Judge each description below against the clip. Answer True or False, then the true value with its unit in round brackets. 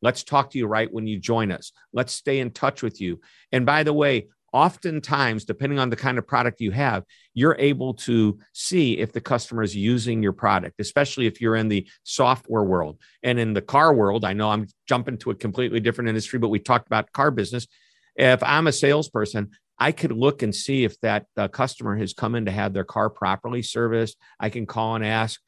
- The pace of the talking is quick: True (215 wpm)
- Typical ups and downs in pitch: True (3.4 semitones)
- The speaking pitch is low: True (115 Hz)